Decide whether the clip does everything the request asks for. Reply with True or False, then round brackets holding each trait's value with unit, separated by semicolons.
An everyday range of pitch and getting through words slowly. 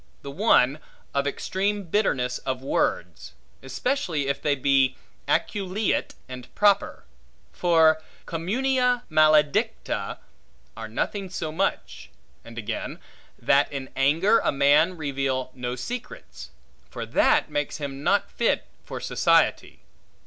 False (6.3 semitones; 115 wpm)